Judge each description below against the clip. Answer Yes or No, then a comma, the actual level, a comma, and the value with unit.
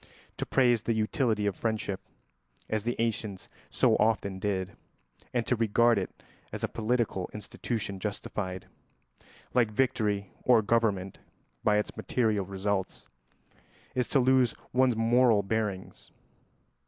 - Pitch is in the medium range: No, low, 110 Hz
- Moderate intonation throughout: Yes, average, 3.0 semitones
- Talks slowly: Yes, slow, 125 wpm